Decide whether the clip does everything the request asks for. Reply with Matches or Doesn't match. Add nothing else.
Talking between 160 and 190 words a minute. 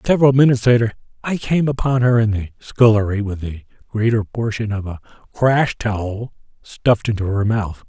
Matches